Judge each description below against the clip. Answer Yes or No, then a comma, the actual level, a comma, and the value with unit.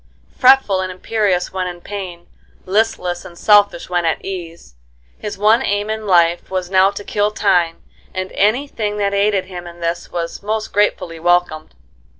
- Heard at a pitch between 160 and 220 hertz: Yes, high, 190 Hz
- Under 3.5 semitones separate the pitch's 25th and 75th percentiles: Yes, average, 2.9 semitones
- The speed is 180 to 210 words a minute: No, average, 165 wpm